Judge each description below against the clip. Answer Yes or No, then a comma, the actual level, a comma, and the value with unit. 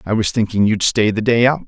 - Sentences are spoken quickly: Yes, fast, 285 wpm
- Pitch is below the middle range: Yes, low, 110 Hz